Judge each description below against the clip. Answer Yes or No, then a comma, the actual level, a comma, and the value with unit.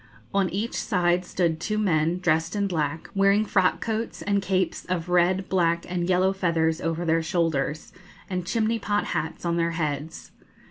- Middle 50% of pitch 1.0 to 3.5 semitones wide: Yes, average, 2.8 semitones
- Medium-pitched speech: Yes, medium, 175 Hz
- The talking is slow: No, average, 170 wpm